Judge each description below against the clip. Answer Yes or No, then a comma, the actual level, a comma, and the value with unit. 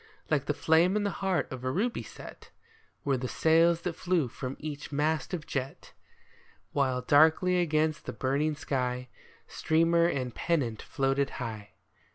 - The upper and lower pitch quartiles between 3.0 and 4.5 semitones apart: Yes, average, 4.2 semitones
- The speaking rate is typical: Yes, average, 155 wpm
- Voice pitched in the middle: Yes, medium, 150 Hz